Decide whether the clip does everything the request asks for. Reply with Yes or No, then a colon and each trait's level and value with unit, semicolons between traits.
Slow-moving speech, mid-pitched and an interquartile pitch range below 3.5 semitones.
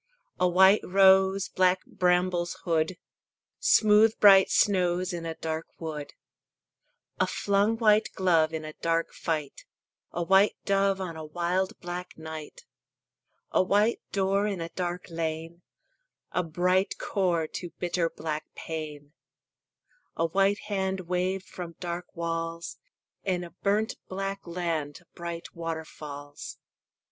Yes: slow, 125 wpm; medium, 180 Hz; narrow, 2.6 semitones